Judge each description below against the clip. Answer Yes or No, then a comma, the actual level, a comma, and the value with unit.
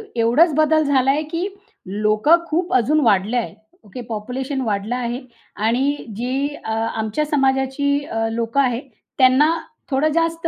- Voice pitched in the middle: No, very high, 265 Hz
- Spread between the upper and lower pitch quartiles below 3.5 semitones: No, average, 4.6 semitones